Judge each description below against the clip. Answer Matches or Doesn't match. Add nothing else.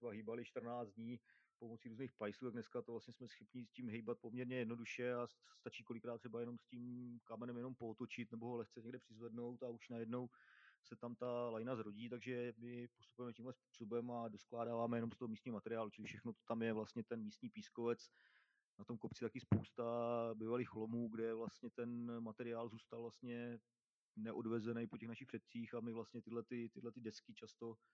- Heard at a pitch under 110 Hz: Doesn't match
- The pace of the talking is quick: Matches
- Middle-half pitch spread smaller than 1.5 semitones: Matches